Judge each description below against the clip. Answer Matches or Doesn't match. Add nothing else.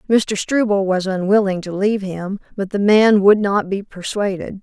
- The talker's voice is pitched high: Matches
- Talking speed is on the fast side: Doesn't match